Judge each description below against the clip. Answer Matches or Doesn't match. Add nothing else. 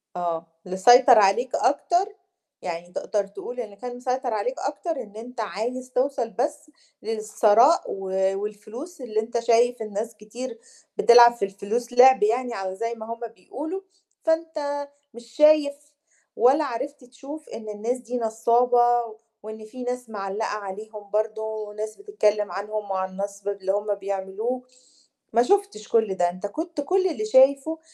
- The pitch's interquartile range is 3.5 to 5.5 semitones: Matches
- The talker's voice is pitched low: Doesn't match